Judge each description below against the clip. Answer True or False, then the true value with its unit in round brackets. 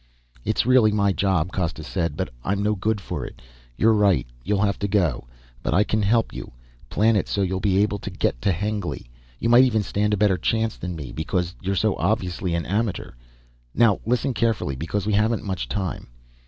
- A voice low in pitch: True (100 Hz)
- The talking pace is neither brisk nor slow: False (210 wpm)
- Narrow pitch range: False (3.1 semitones)